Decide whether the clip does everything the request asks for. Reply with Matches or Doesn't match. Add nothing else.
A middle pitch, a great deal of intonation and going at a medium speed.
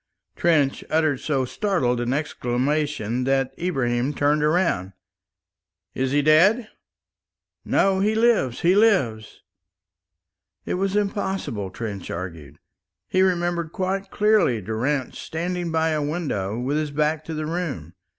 Doesn't match